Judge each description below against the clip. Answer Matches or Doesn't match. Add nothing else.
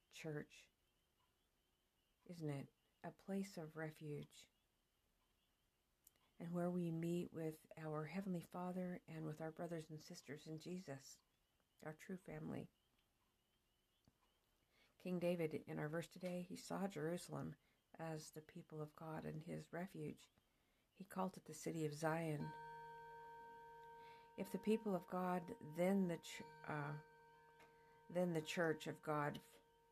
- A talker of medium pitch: Matches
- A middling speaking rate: Doesn't match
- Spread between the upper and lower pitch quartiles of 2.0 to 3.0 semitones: Matches